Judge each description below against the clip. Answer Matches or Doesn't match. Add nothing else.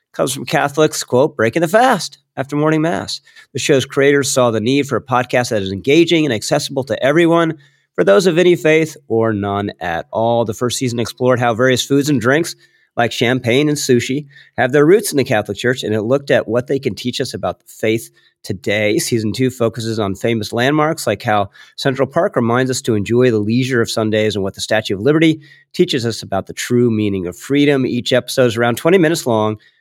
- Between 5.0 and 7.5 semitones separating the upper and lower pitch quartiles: Doesn't match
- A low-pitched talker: Matches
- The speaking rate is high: Matches